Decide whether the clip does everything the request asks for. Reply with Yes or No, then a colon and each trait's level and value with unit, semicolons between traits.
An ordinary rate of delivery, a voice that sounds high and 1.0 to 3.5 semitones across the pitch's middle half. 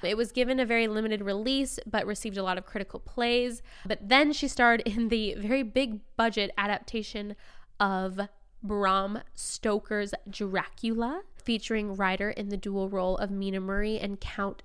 Yes: average, 160 wpm; high, 215 Hz; average, 2.7 semitones